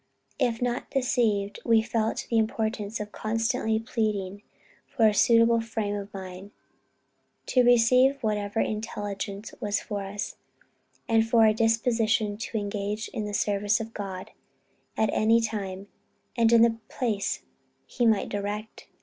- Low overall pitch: No, high, 220 Hz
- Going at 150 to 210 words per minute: No, average, 140 wpm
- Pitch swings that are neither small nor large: No, narrow, 1.9 semitones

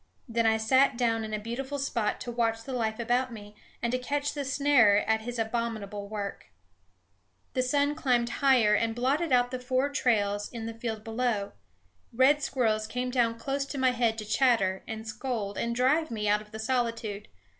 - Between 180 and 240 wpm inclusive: Yes, average, 190 wpm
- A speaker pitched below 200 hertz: No, high, 235 Hz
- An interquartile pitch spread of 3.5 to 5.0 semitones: No, average, 2.8 semitones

